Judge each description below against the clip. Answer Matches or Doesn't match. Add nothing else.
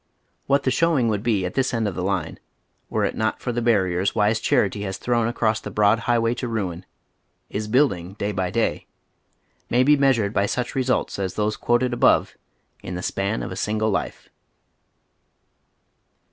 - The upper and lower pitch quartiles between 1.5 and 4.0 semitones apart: Matches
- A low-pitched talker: Matches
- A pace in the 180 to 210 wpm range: Matches